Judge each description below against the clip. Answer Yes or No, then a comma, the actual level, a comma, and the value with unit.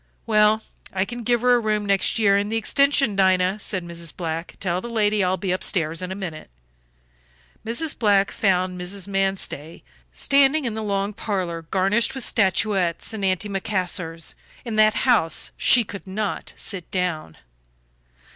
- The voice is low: No, high, 195 Hz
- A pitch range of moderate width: Yes, average, 3.1 semitones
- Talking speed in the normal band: Yes, average, 155 wpm